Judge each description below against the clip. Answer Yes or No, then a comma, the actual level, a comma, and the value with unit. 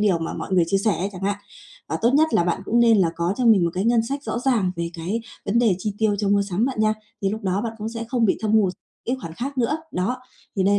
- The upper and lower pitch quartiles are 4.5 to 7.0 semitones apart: No, average, 3.7 semitones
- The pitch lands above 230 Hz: No, high, 210 Hz